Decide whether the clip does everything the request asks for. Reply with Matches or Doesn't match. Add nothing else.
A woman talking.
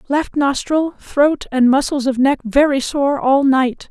Matches